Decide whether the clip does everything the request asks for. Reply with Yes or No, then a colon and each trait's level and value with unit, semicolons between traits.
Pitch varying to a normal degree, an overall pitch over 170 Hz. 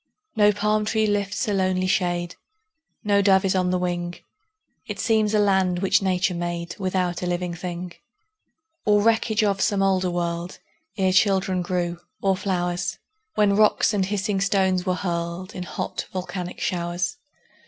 No: narrow, 2.2 semitones; medium, 185 Hz